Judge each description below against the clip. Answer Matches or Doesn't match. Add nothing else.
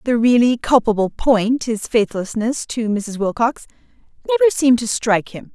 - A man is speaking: Doesn't match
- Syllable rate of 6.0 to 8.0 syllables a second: Doesn't match